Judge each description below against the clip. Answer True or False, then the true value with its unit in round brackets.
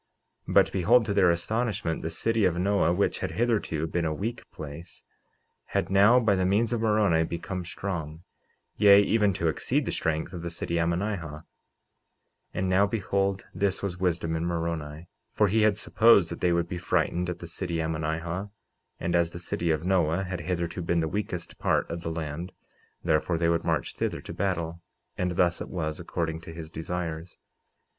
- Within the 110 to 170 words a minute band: False (190 wpm)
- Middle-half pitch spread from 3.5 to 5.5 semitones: False (3.1 semitones)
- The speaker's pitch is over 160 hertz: False (85 Hz)